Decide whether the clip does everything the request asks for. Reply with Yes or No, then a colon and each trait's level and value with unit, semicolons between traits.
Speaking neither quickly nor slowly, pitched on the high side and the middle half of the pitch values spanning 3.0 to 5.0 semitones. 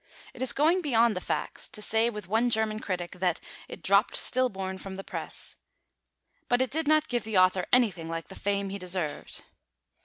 Yes: average, 190 wpm; high, 210 Hz; average, 4.5 semitones